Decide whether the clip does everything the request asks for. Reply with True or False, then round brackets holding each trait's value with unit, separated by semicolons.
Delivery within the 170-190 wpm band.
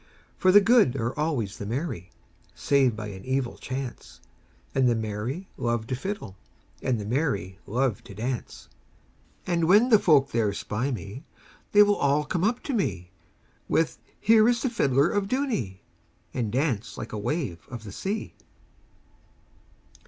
False (160 wpm)